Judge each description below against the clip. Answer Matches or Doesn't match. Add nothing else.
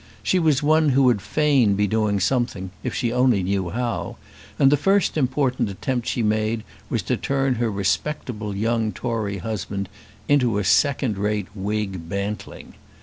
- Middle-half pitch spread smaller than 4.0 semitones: Doesn't match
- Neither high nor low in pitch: Doesn't match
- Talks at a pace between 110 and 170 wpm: Matches